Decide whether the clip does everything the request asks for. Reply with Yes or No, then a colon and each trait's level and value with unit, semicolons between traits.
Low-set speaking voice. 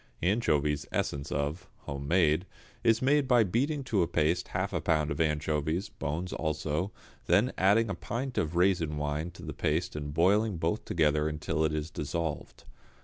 Yes: very low, 85 Hz